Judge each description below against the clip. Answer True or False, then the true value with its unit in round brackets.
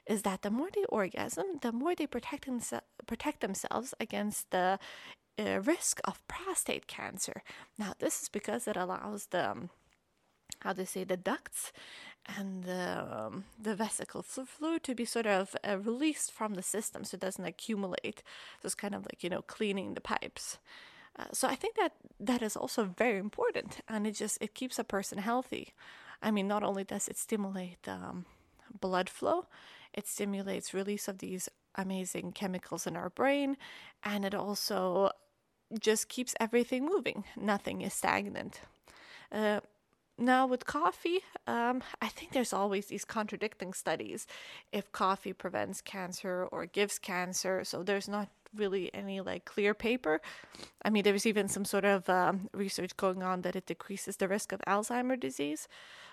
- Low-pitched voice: False (205 Hz)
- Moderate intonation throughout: True (4.1 semitones)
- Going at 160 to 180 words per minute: True (170 wpm)